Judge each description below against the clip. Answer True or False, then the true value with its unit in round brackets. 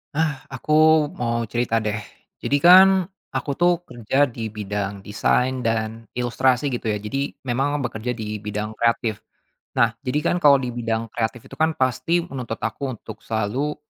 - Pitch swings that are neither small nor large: True (3.1 semitones)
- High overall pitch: False (120 Hz)